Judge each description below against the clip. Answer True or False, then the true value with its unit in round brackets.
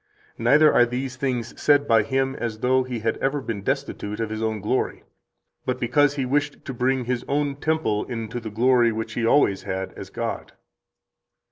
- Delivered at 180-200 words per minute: True (190 wpm)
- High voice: False (125 Hz)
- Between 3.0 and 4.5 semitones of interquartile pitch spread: True (3.3 semitones)